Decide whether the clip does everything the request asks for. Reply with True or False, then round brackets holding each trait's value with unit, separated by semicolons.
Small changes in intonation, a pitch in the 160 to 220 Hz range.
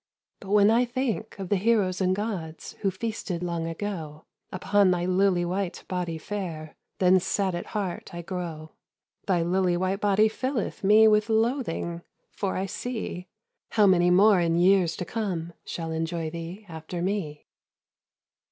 False (3.2 semitones; 185 Hz)